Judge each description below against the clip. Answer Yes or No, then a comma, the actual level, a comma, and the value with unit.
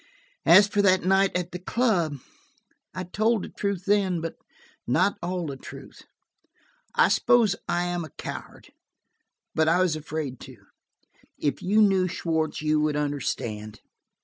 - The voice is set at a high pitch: No, medium, 175 Hz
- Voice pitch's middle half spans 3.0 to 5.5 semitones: Yes, average, 4.2 semitones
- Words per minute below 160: Yes, average, 150 wpm